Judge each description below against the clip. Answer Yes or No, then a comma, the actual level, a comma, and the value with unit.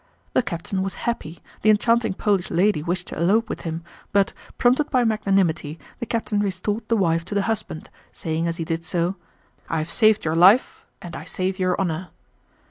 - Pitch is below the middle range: No, high, 190 Hz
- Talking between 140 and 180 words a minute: No, average, 190 wpm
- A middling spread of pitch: Yes, average, 4.3 semitones